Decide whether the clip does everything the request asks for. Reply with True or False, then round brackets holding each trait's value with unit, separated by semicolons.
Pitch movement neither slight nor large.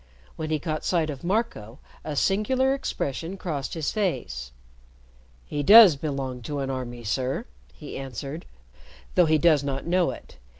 True (4.9 semitones)